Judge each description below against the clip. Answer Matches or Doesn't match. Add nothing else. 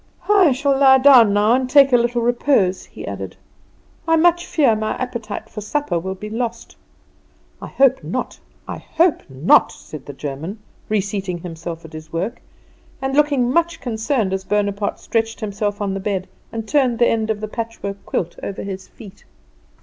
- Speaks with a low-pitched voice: Doesn't match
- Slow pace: Doesn't match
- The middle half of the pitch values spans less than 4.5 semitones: Doesn't match